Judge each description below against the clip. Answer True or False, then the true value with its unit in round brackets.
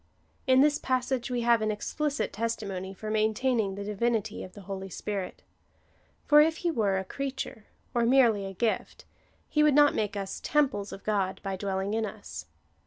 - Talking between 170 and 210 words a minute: True (175 wpm)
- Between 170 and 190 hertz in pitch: False (215 Hz)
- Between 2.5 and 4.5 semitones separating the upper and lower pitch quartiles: False (4.9 semitones)